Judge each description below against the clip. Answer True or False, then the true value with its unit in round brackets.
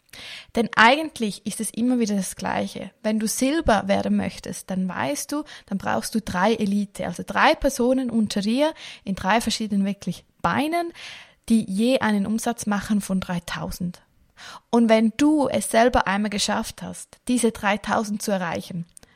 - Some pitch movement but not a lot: True (3.2 semitones)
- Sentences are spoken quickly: False (155 wpm)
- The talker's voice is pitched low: False (220 Hz)